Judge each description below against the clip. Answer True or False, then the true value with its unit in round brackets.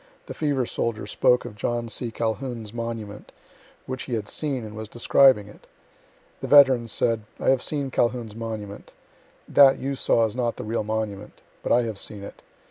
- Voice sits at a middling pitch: False (115 Hz)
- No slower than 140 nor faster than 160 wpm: False (180 wpm)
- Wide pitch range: False (2.8 semitones)